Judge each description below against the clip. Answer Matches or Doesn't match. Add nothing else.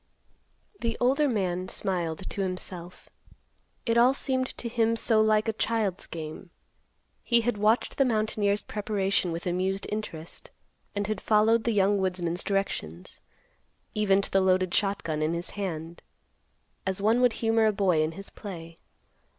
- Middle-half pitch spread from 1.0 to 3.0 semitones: Doesn't match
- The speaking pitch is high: Matches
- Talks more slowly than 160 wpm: Matches